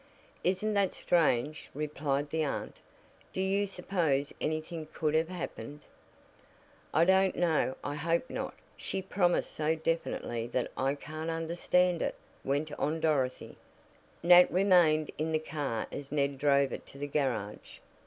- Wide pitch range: No, average, 3.6 semitones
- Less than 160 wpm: Yes, average, 145 wpm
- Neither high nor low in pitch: Yes, medium, 155 Hz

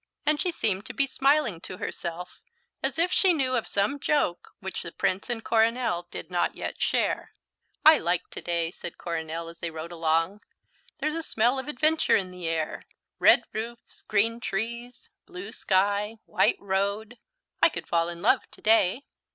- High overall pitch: Yes, high, 205 Hz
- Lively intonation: Yes, wide, 6.1 semitones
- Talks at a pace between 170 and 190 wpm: Yes, average, 175 wpm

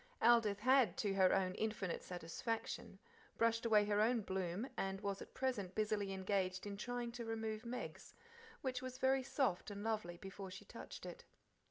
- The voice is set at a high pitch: Yes, high, 215 Hz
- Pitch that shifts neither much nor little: Yes, average, 3.6 semitones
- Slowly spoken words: No, average, 170 wpm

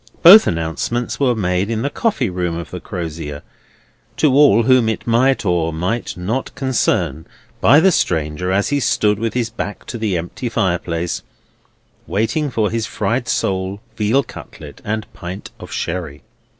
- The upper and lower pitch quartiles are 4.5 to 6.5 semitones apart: Yes, wide, 5.5 semitones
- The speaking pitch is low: Yes, low, 105 Hz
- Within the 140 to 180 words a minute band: Yes, average, 160 wpm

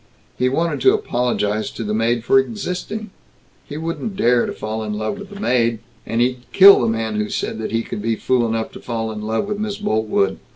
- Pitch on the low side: Yes, low, 120 Hz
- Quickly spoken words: Yes, fast, 215 wpm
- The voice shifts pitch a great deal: Yes, wide, 8.5 semitones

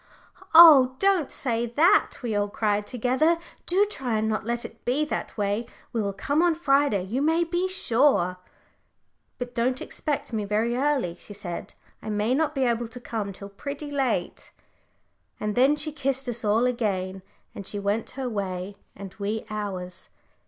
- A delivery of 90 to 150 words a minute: No, average, 175 wpm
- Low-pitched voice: No, high, 235 Hz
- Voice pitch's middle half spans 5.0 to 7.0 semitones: Yes, wide, 5.5 semitones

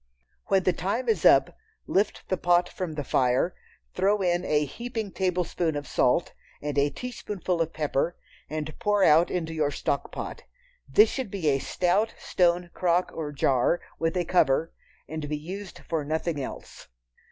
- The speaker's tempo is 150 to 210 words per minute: Yes, average, 165 wpm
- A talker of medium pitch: Yes, medium, 170 Hz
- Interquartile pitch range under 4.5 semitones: Yes, average, 3.9 semitones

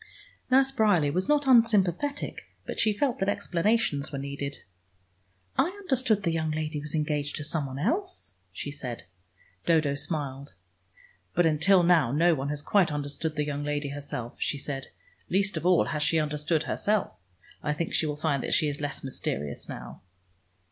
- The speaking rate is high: No, average, 170 wpm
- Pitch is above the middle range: No, medium, 155 Hz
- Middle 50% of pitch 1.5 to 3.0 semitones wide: No, average, 5.0 semitones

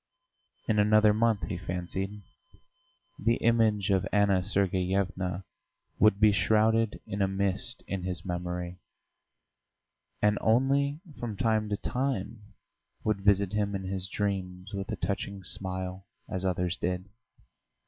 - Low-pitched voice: Yes, low, 100 Hz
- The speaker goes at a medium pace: No, slow, 130 wpm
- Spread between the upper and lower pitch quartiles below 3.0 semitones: Yes, narrow, 2.4 semitones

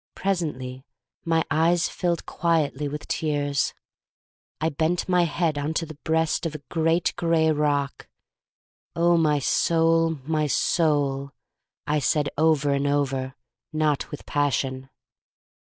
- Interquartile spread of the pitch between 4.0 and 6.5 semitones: No, narrow, 2.5 semitones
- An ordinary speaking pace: No, slow, 120 wpm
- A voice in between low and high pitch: Yes, medium, 155 Hz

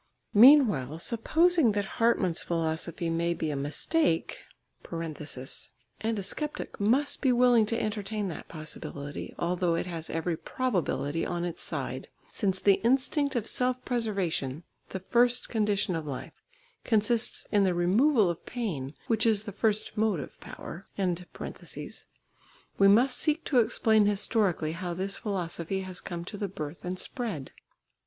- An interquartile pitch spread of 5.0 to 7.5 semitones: Yes, wide, 5.4 semitones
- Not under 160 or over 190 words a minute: No, average, 140 wpm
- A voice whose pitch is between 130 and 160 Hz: No, high, 195 Hz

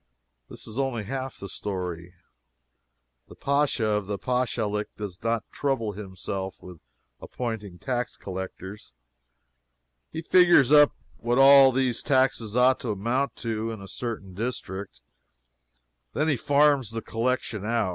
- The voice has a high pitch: No, low, 115 Hz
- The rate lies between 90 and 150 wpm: Yes, slow, 135 wpm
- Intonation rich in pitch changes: No, average, 4.7 semitones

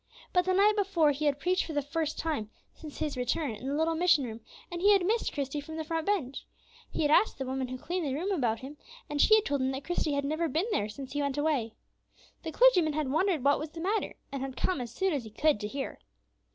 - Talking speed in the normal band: No, fast, 260 wpm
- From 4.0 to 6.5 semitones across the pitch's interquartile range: Yes, average, 4.4 semitones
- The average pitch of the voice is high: Yes, very high, 300 Hz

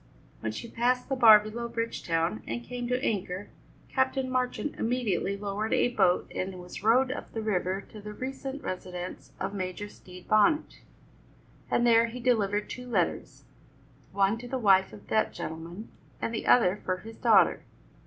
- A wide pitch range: No, average, 4.7 semitones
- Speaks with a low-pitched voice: No, high, 215 Hz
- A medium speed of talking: Yes, average, 165 wpm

